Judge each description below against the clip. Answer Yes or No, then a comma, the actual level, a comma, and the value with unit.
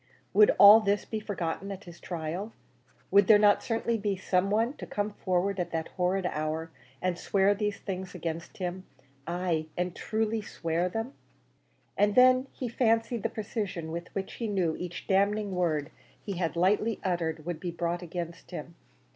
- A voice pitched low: No, high, 190 Hz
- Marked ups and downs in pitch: No, average, 3.3 semitones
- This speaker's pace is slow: No, average, 170 wpm